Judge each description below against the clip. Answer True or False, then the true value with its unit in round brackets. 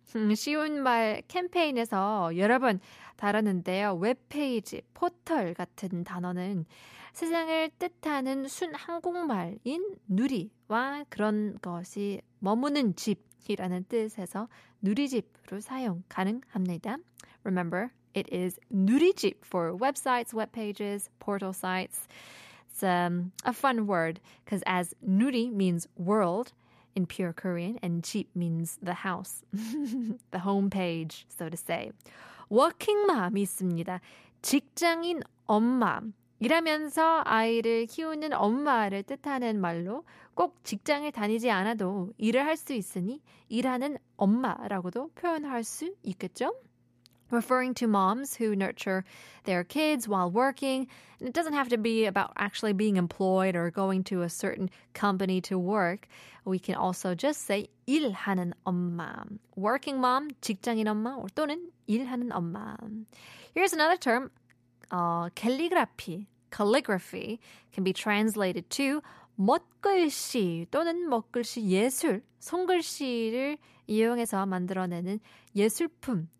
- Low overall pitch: False (215 Hz)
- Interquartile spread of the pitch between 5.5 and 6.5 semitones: True (5.9 semitones)